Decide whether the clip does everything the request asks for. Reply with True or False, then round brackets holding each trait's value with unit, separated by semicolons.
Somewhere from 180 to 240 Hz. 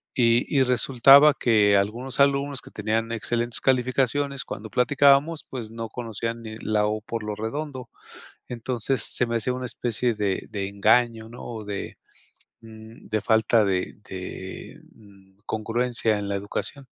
False (115 Hz)